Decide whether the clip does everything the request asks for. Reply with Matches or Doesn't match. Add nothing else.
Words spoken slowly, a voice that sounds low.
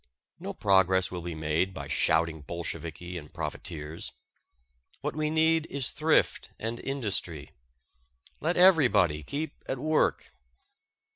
Matches